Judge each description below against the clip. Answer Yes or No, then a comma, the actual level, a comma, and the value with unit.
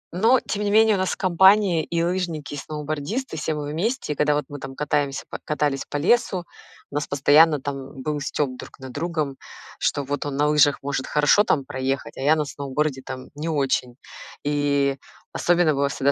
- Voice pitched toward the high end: No, medium, 150 Hz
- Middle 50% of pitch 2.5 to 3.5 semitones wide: Yes, average, 3.0 semitones